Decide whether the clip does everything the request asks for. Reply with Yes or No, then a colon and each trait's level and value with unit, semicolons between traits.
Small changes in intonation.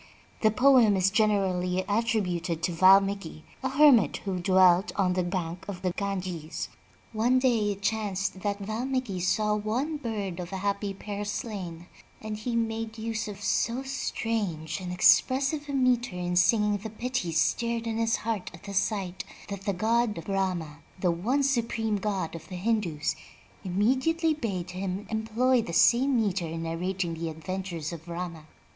No: average, 4.1 semitones